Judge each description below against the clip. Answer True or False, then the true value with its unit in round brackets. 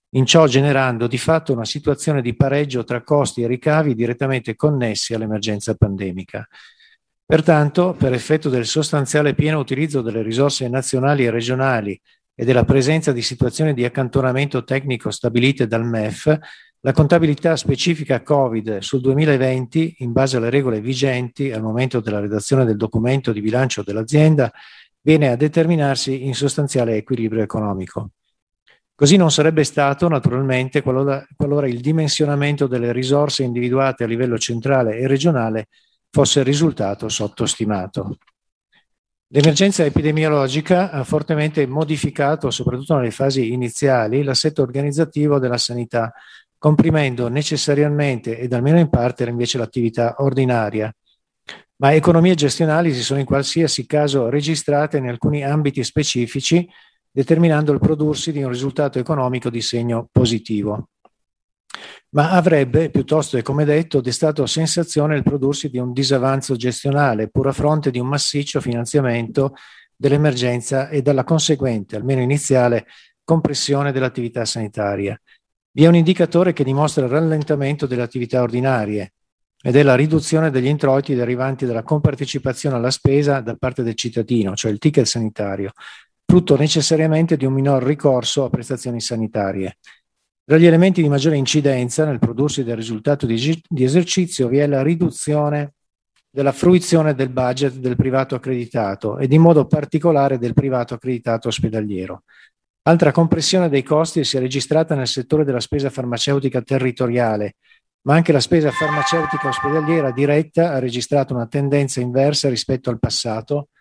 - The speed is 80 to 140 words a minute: True (135 wpm)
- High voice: False (135 Hz)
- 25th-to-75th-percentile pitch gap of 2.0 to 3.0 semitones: False (3.6 semitones)